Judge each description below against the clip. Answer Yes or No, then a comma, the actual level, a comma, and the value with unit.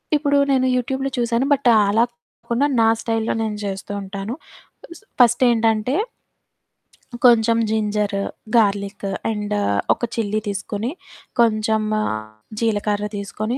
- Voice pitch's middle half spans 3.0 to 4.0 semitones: No, narrow, 2.5 semitones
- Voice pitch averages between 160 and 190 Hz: No, high, 220 Hz